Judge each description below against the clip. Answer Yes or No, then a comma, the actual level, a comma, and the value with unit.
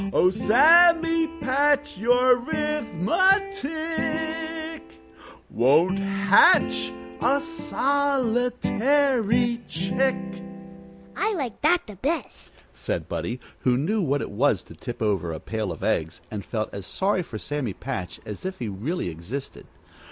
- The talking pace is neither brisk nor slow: No, slow, 120 wpm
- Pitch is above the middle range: Yes, high, 235 Hz